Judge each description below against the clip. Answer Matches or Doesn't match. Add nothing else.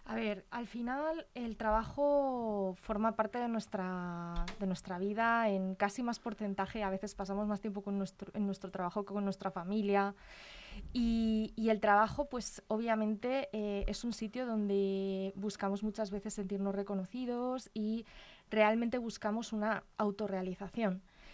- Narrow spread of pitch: Matches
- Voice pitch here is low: Doesn't match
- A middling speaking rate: Matches